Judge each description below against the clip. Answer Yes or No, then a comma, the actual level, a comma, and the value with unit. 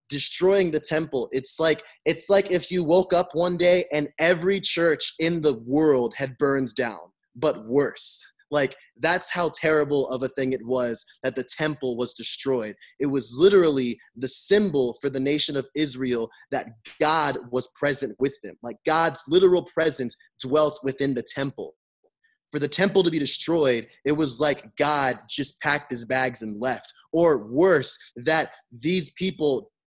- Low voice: No, medium, 145 Hz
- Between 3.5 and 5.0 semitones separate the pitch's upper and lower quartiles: Yes, average, 4.1 semitones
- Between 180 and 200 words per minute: No, average, 165 wpm